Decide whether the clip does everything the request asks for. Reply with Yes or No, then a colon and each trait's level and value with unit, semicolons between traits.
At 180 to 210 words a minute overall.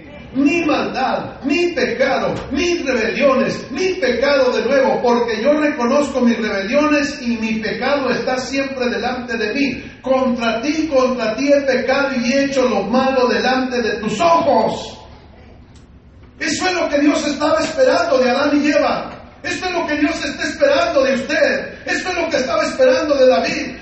No: average, 165 wpm